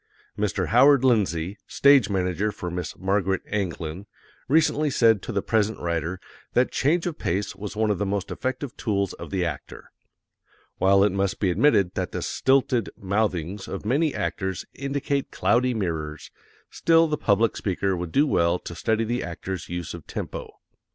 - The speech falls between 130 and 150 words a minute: No, average, 165 wpm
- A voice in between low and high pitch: No, low, 100 Hz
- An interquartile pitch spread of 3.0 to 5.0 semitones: No, wide, 5.4 semitones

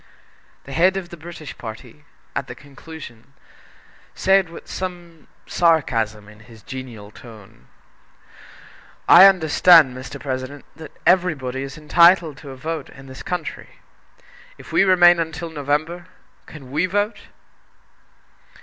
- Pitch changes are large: No, average, 5.0 semitones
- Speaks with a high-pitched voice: No, medium, 150 Hz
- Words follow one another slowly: Yes, slow, 125 wpm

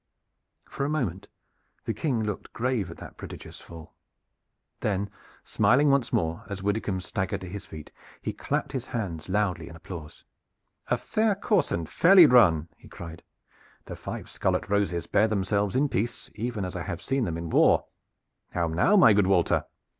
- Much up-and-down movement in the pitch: Yes, wide, 5.9 semitones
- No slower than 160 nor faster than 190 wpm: Yes, average, 170 wpm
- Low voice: Yes, low, 100 Hz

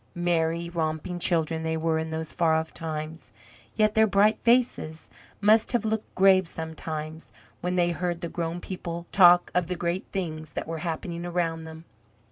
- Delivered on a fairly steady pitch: Yes, narrow, 2.0 semitones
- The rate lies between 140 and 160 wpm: No, average, 170 wpm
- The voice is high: No, medium, 170 Hz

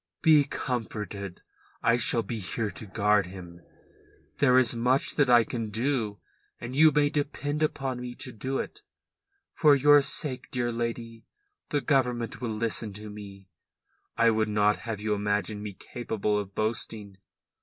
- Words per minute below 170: Yes, average, 155 wpm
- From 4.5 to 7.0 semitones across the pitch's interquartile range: No, average, 3.7 semitones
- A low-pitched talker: Yes, low, 115 Hz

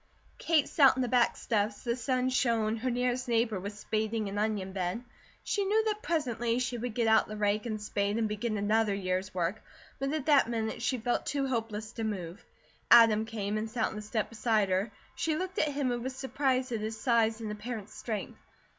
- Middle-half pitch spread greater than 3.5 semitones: No, average, 3.1 semitones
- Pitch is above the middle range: Yes, high, 225 Hz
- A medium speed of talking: No, fast, 210 wpm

